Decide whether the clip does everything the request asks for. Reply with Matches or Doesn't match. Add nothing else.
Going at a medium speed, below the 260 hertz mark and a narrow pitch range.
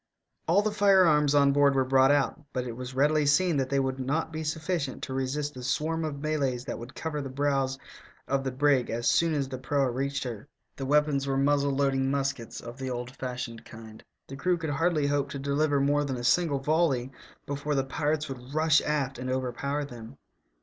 Doesn't match